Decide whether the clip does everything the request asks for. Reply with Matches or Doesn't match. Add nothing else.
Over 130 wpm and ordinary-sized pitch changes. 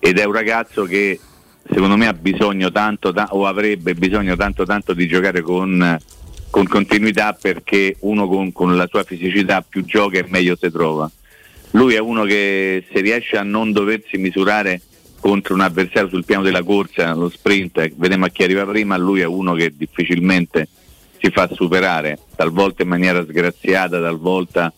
Doesn't match